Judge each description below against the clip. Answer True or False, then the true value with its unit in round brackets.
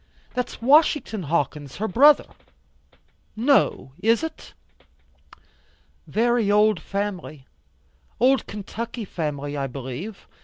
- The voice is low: False (210 Hz)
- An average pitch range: False (7.5 semitones)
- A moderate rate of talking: False (90 wpm)